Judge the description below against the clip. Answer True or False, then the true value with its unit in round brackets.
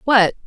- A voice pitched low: False (225 Hz)